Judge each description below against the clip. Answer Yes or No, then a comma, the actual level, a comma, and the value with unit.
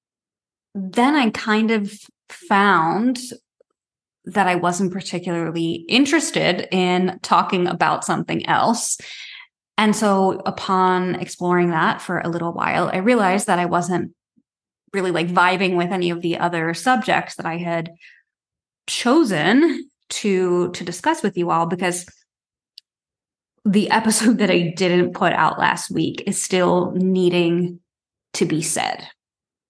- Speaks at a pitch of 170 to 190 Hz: Yes, medium, 185 Hz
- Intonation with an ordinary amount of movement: Yes, average, 3.7 semitones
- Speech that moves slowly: Yes, slow, 130 wpm